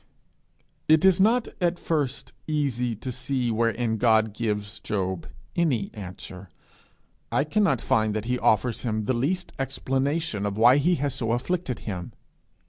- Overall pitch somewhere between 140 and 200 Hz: No, low, 125 Hz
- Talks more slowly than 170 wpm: Yes, average, 145 wpm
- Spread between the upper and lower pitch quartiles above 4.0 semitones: Yes, average, 5.1 semitones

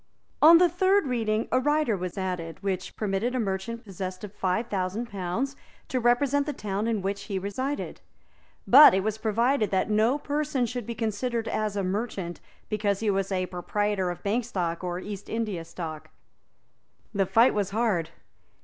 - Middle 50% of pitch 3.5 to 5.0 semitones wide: Yes, average, 4.2 semitones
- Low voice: No, high, 210 Hz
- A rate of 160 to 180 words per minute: Yes, average, 175 wpm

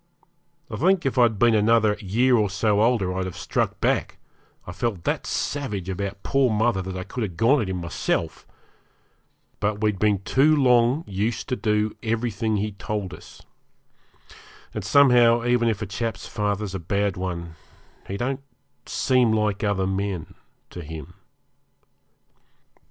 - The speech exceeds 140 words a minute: Yes, average, 155 wpm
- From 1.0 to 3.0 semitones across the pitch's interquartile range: No, average, 3.6 semitones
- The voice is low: Yes, low, 105 Hz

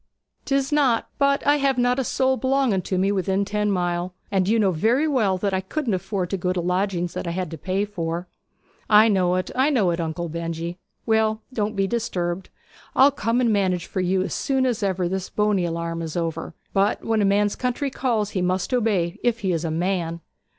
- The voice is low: No, high, 195 Hz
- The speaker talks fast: Yes, fast, 215 wpm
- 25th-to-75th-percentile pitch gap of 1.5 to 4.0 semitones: No, average, 4.4 semitones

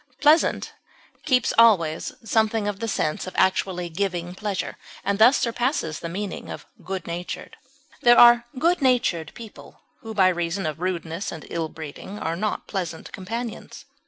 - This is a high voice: Yes, high, 195 Hz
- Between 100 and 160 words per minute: Yes, average, 155 wpm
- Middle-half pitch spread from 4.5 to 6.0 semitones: Yes, average, 5.2 semitones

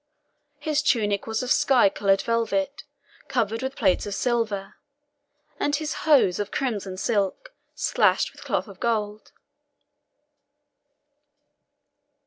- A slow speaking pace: Yes, slow, 115 wpm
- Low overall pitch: No, high, 225 Hz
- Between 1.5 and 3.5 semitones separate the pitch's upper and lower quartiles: No, average, 4.9 semitones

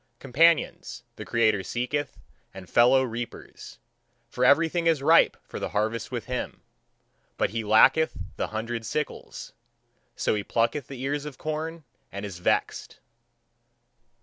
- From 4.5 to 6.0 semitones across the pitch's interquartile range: Yes, average, 5.0 semitones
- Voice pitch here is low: Yes, low, 125 Hz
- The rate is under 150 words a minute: Yes, slow, 135 wpm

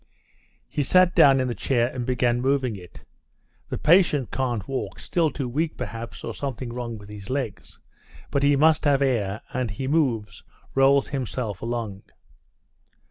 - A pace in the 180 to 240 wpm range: No, average, 155 wpm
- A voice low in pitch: Yes, low, 130 Hz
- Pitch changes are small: No, average, 3.4 semitones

